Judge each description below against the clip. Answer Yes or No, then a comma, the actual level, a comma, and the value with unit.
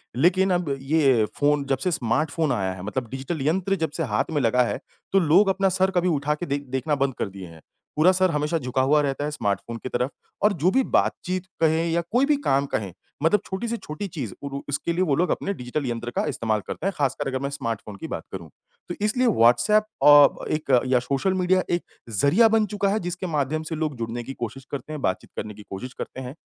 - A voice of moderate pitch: Yes, medium, 150 Hz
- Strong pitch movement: Yes, wide, 6.0 semitones